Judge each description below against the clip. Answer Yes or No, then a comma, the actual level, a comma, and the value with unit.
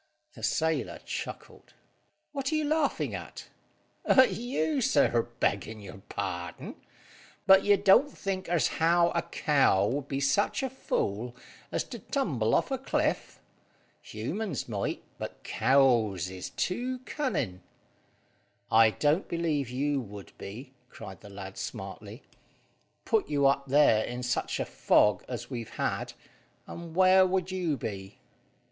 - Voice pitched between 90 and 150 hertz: Yes, medium, 140 Hz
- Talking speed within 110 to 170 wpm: Yes, average, 140 wpm